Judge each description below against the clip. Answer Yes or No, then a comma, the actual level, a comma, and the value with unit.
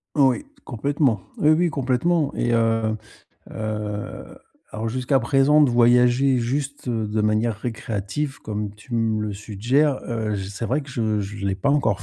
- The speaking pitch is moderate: No, low, 115 Hz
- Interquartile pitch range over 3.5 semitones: Yes, average, 4.2 semitones